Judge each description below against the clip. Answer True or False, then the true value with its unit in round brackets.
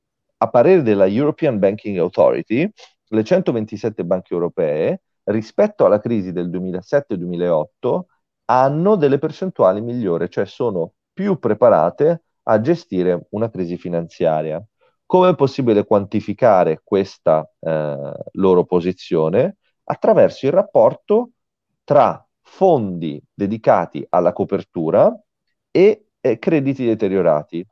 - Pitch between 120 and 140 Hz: False (110 Hz)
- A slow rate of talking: True (105 wpm)